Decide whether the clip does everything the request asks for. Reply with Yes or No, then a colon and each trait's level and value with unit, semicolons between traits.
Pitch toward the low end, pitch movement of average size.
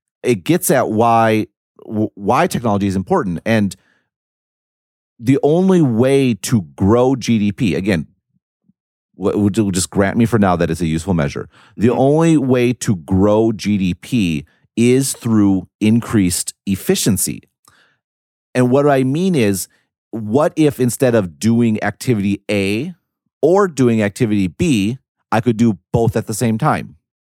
Yes: low, 115 Hz; average, 4.1 semitones